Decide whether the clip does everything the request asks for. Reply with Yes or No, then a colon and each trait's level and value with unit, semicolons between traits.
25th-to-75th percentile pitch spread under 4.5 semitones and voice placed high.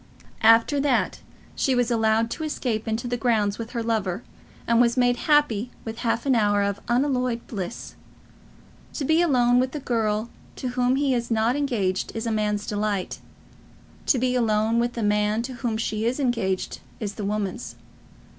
Yes: average, 2.7 semitones; high, 230 Hz